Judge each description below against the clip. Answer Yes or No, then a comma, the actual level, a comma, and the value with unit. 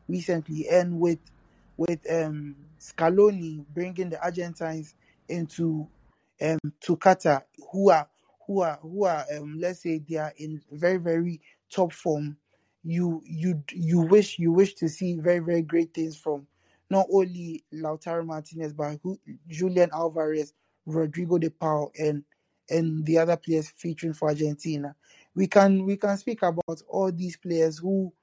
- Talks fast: No, average, 150 wpm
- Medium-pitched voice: Yes, medium, 165 Hz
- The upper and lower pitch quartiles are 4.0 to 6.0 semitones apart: No, narrow, 2.4 semitones